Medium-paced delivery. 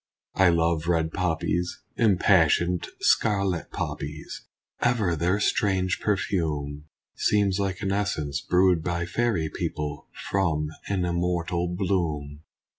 No: slow, 110 wpm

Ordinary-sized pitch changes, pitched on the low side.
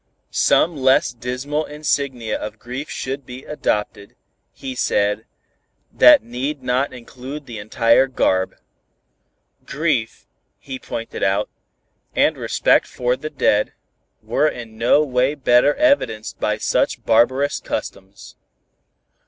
Yes: average, 3.6 semitones; low, 125 Hz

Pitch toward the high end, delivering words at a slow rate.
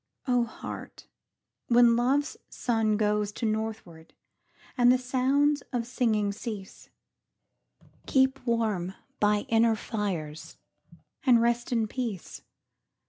Yes: high, 230 Hz; slow, 105 wpm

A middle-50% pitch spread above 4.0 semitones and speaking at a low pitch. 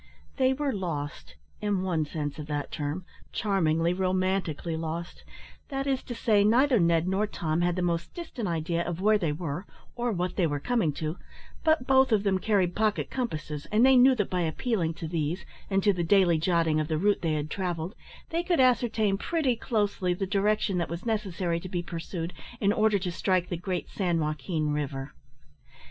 No: average, 4.5 semitones; medium, 185 Hz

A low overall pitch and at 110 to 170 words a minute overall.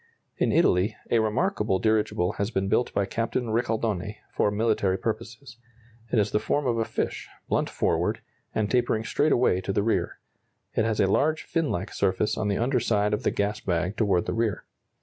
No: low, 110 Hz; average, 190 wpm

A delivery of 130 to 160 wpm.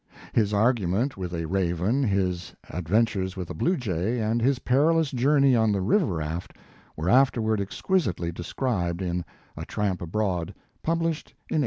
Yes: average, 155 wpm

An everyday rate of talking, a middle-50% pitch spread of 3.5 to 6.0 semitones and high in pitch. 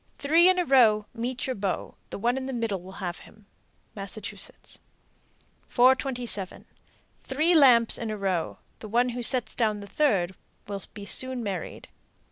Yes: average, 160 wpm; average, 4.4 semitones; high, 230 Hz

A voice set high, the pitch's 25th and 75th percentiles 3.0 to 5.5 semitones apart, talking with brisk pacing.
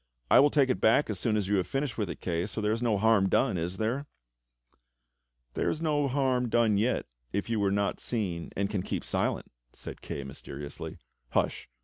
No: low, 110 Hz; average, 4.4 semitones; fast, 210 wpm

